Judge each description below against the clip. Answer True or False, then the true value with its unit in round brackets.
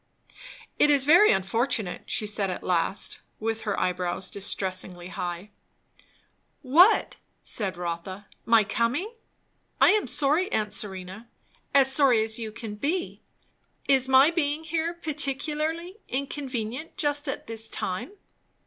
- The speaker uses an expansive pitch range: True (6.9 semitones)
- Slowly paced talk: True (125 wpm)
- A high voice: True (240 Hz)